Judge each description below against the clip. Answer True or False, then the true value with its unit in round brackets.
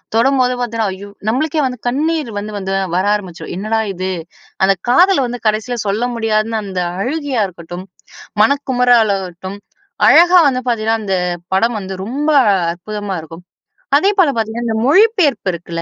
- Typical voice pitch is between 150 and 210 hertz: False (225 Hz)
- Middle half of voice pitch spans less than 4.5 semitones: False (5.1 semitones)